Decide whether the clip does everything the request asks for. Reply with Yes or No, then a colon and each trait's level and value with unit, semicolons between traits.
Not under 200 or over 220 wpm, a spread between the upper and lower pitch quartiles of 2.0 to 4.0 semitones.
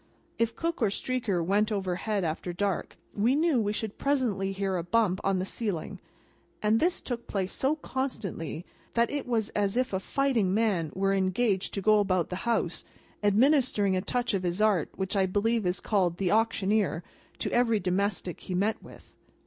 No: average, 180 wpm; average, 3.6 semitones